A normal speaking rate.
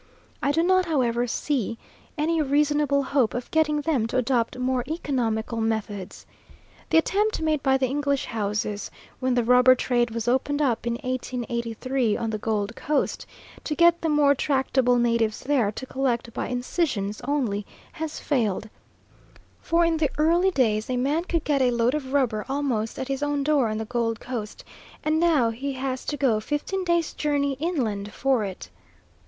Yes: average, 170 wpm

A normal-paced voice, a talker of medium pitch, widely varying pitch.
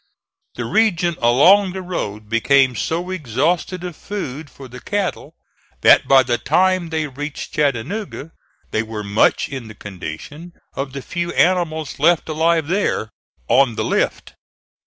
Yes: average, 145 wpm; medium, 150 Hz; wide, 5.8 semitones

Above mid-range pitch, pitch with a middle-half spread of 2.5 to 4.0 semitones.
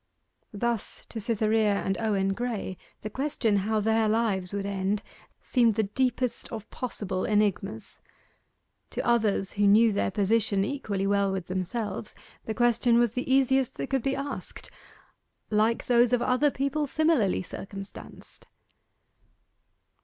Yes: high, 220 Hz; average, 3.3 semitones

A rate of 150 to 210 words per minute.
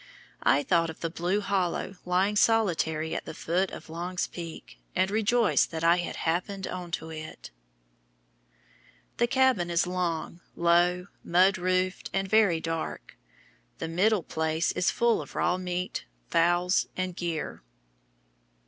No: average, 140 wpm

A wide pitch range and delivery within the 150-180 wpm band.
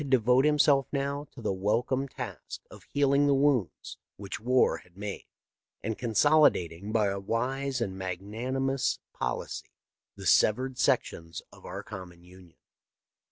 No: wide, 5.8 semitones; average, 140 wpm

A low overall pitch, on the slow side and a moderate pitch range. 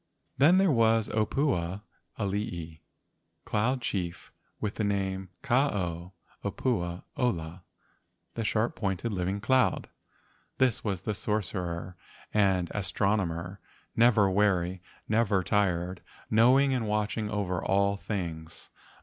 Yes: low, 100 Hz; slow, 115 wpm; average, 3.7 semitones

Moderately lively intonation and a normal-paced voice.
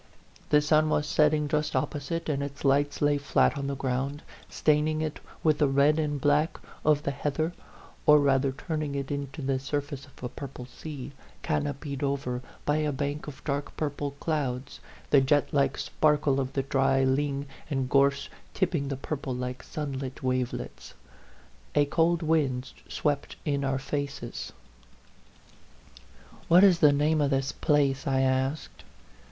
No: narrow, 1.9 semitones; average, 160 wpm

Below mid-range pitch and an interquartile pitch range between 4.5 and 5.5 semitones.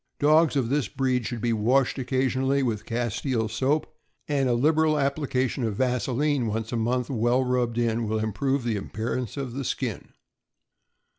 No: low, 125 Hz; average, 2.9 semitones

